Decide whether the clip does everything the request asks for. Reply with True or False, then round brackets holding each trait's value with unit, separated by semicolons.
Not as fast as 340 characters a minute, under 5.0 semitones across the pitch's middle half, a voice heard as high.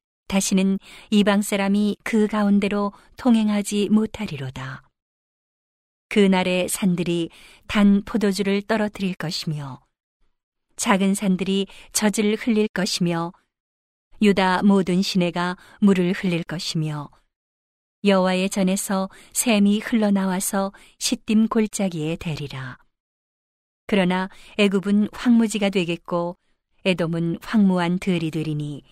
True (235 characters per minute; 2.9 semitones; 195 Hz)